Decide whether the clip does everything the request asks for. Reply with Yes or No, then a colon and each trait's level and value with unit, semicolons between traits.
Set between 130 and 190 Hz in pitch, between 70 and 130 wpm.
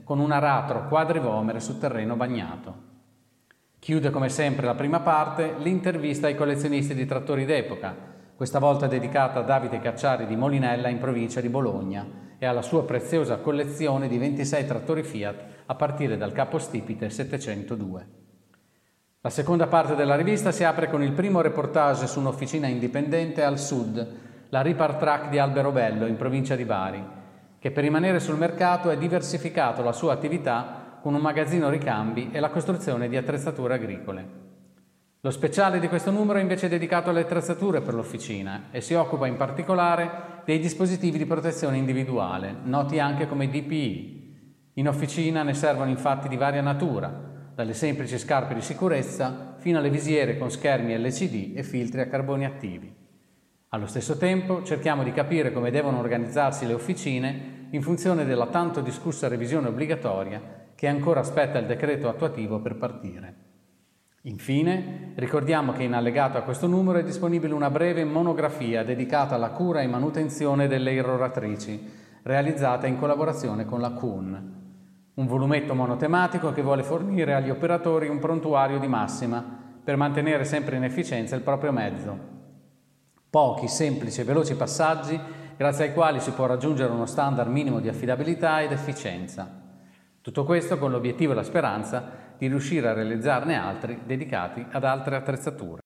No: medium, 140 Hz; average, 155 wpm